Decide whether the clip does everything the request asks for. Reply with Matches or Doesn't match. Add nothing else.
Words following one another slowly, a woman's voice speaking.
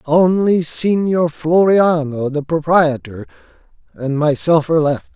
Doesn't match